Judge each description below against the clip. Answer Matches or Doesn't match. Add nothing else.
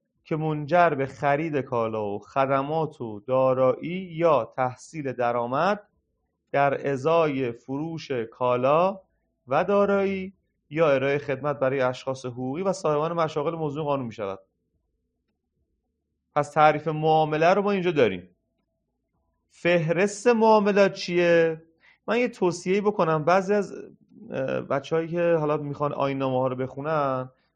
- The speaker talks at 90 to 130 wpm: Matches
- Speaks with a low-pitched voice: Doesn't match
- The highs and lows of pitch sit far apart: Doesn't match